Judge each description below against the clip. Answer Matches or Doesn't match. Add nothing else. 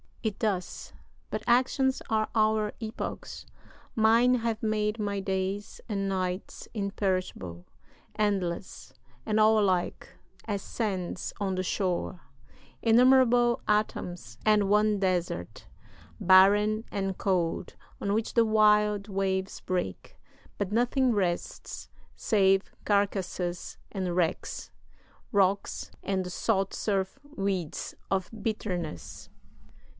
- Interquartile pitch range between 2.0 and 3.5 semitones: Matches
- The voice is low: Doesn't match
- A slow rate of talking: Matches